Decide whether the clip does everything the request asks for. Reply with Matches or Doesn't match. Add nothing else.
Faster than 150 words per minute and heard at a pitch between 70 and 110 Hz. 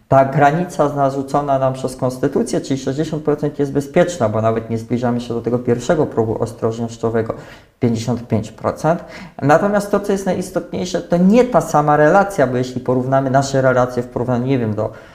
Doesn't match